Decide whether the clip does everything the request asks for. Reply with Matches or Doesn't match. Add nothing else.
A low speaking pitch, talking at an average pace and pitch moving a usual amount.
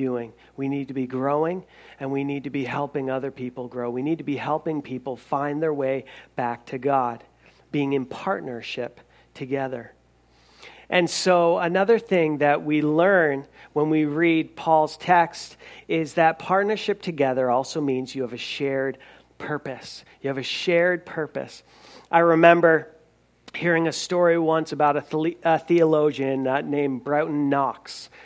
Doesn't match